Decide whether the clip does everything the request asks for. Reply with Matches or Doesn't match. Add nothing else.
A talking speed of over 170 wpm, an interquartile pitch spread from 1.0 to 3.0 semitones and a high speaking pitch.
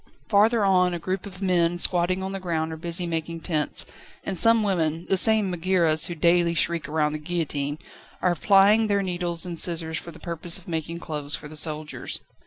Doesn't match